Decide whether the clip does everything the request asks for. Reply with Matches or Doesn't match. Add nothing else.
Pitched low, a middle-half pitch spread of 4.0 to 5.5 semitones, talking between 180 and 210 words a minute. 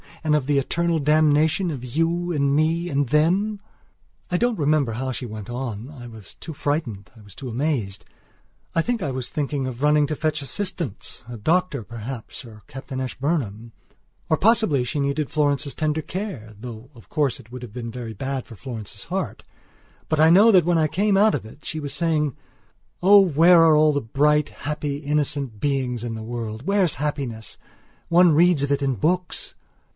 Doesn't match